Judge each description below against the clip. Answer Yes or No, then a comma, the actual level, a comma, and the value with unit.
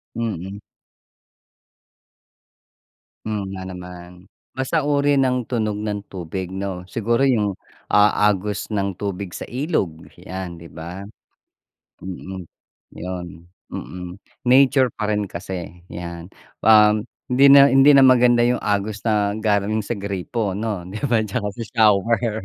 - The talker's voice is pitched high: No, low, 105 Hz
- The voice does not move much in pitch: No, average, 4.1 semitones